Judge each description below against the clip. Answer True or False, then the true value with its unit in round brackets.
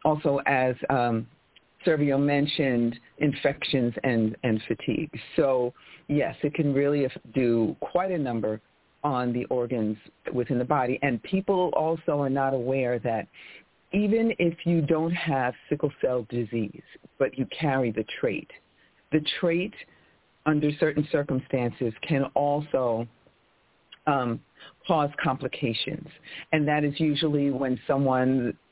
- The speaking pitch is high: False (135 Hz)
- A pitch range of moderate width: True (3.6 semitones)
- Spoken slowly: True (125 wpm)